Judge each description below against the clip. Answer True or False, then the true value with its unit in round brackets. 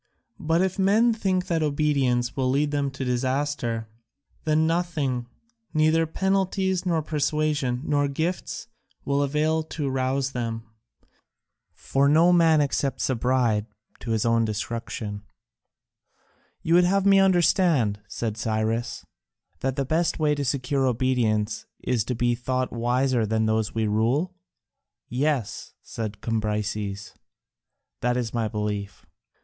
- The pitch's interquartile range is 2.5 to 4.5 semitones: False (5.4 semitones)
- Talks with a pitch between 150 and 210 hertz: False (135 Hz)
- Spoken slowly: True (130 wpm)